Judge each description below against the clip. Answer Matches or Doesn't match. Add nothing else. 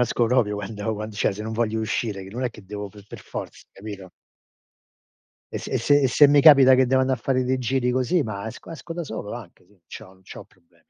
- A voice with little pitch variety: Doesn't match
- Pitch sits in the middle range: Doesn't match